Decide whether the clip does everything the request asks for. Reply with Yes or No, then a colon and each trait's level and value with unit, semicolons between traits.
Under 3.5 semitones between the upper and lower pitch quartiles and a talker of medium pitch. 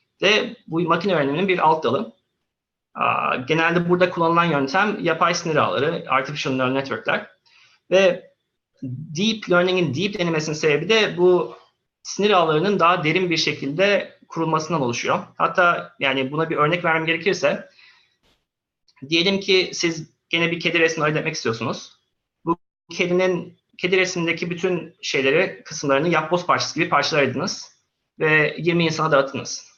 Yes: average, 2.9 semitones; medium, 170 Hz